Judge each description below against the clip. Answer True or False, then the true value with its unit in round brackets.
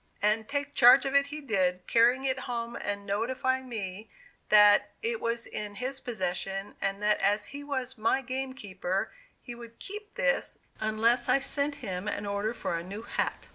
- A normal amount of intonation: True (4.5 semitones)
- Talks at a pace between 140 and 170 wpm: False (180 wpm)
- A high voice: True (230 Hz)